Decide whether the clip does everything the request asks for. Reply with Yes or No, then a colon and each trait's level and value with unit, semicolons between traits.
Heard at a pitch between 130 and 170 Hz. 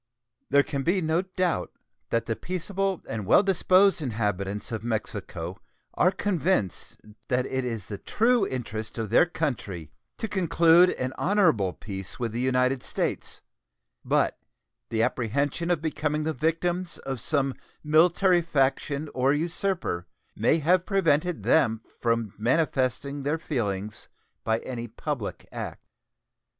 Yes: medium, 140 Hz